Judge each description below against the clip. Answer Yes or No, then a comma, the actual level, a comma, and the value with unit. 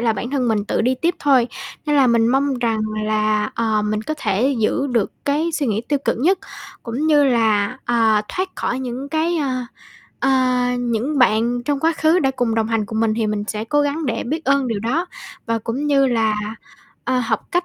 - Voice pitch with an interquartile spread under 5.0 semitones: Yes, average, 4.2 semitones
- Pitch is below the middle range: No, high, 245 Hz